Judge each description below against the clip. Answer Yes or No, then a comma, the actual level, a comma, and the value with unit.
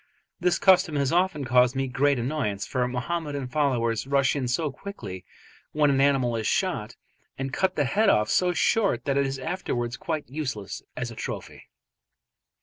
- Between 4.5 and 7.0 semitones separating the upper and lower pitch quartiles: No, average, 4.1 semitones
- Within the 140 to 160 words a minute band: No, average, 170 wpm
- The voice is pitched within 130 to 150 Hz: Yes, low, 135 Hz